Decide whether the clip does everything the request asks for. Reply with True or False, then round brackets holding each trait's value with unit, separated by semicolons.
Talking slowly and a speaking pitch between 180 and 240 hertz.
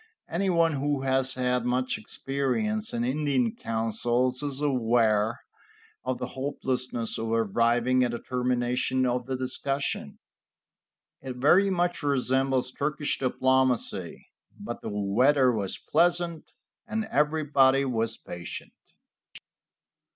False (110 wpm; 130 Hz)